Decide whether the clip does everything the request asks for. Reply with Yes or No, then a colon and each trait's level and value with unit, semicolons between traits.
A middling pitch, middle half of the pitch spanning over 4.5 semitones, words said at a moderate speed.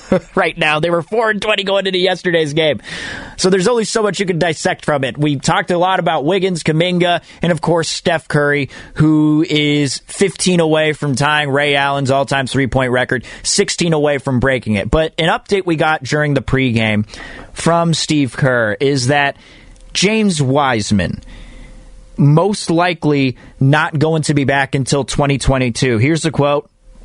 No: medium, 150 Hz; average, 4.2 semitones; average, 170 wpm